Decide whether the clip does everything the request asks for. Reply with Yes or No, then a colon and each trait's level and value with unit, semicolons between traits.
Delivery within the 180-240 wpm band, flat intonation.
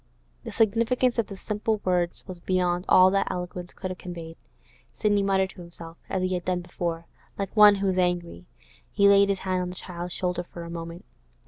Yes: fast, 205 wpm; narrow, 2.2 semitones